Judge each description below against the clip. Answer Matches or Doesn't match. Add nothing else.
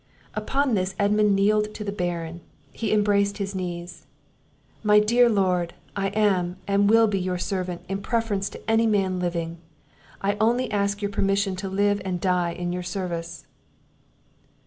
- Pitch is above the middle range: Matches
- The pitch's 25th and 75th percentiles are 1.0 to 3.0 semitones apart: Matches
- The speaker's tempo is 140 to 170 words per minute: Matches